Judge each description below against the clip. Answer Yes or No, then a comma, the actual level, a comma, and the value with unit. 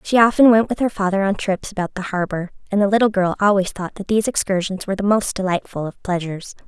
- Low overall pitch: No, high, 195 Hz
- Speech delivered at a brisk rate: Yes, fast, 235 wpm